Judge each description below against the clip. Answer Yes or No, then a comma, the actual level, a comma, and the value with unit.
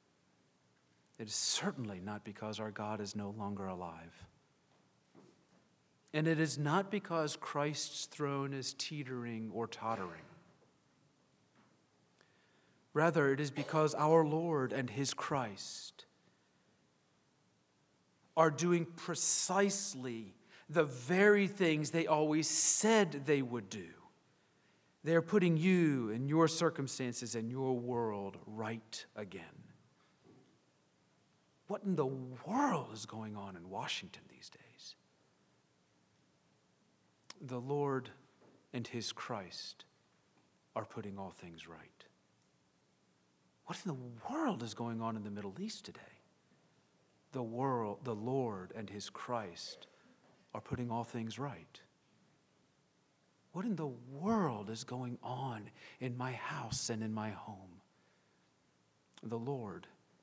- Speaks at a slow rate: Yes, slow, 115 wpm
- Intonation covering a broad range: Yes, wide, 6.4 semitones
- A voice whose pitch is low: Yes, low, 125 Hz